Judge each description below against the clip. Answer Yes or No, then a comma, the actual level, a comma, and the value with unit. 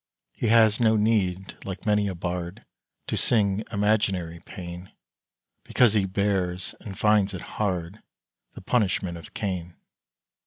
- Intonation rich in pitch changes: No, average, 2.9 semitones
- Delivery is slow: Yes, slow, 130 wpm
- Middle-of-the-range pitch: No, very low, 95 Hz